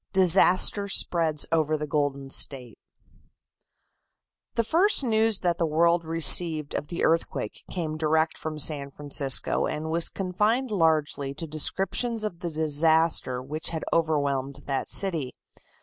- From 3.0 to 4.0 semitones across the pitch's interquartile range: Yes, average, 3.4 semitones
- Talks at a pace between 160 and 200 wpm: No, slow, 135 wpm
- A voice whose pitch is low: No, medium, 160 Hz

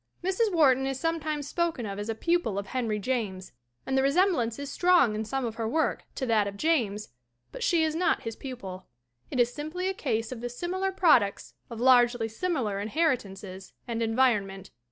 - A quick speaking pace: No, average, 190 wpm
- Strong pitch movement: Yes, wide, 6.6 semitones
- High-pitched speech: Yes, very high, 250 Hz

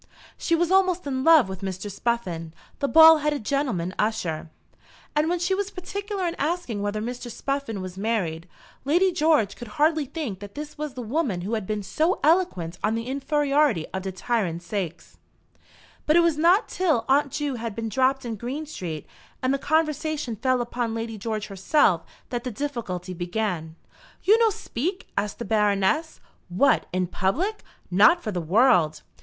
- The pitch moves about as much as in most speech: No, wide, 7.6 semitones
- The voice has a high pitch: Yes, high, 240 Hz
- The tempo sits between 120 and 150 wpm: No, average, 175 wpm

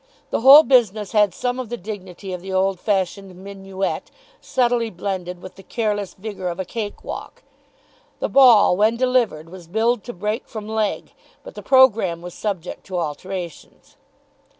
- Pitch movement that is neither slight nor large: Yes, average, 3.6 semitones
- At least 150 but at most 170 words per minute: Yes, average, 165 wpm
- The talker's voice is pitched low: No, high, 200 Hz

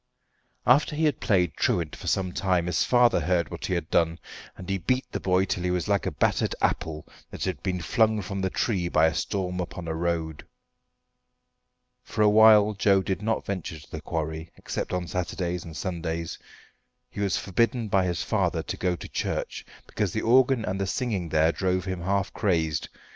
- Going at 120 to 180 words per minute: No, average, 195 wpm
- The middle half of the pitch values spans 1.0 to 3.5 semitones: Yes, average, 3.1 semitones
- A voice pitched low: Yes, very low, 90 Hz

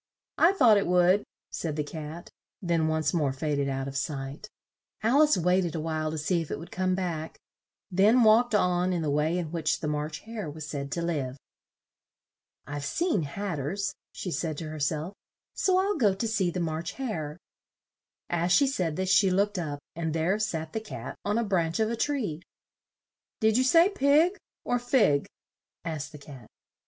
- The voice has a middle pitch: Yes, medium, 175 Hz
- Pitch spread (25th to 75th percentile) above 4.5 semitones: Yes, wide, 5.6 semitones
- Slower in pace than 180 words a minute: No, average, 195 wpm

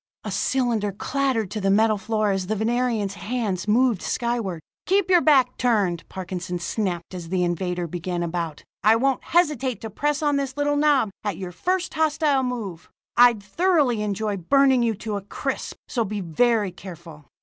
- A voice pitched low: No, high, 215 Hz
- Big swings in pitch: Yes, wide, 5.8 semitones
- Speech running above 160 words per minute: Yes, average, 170 wpm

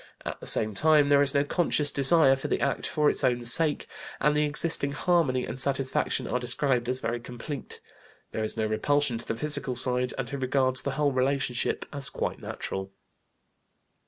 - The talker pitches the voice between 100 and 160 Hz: Yes, low, 135 Hz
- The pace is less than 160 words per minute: No, average, 190 wpm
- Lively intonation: No, average, 2.7 semitones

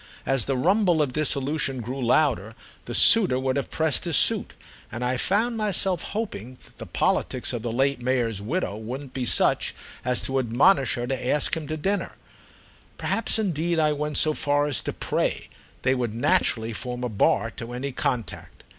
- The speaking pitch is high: No, low, 135 Hz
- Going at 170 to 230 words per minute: Yes, average, 180 wpm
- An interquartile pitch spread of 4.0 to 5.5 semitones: Yes, average, 4.3 semitones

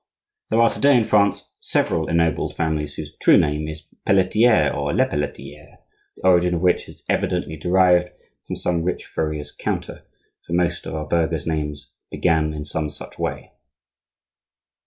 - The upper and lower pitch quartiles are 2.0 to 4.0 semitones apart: Yes, average, 3.1 semitones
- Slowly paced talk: No, average, 155 wpm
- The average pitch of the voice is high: No, very low, 85 Hz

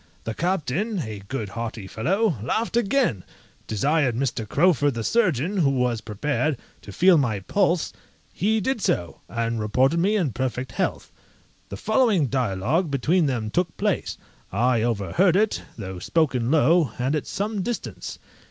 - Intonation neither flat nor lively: No, wide, 7.9 semitones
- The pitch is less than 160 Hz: Yes, medium, 140 Hz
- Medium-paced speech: Yes, average, 150 wpm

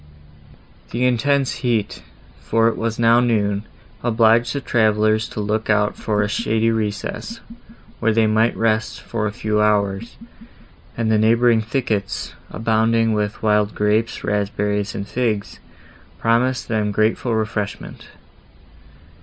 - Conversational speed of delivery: No, slow, 130 wpm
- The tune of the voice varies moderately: No, narrow, 1.6 semitones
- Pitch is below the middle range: Yes, low, 110 Hz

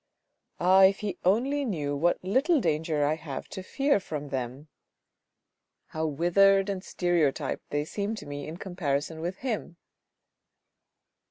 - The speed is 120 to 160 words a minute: Yes, average, 140 wpm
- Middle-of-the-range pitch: Yes, medium, 175 Hz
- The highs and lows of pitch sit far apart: No, average, 4.8 semitones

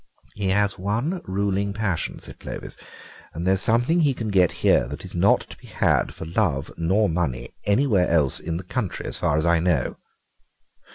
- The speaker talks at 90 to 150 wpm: No, average, 190 wpm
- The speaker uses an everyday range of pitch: Yes, average, 3.9 semitones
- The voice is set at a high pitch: No, very low, 95 Hz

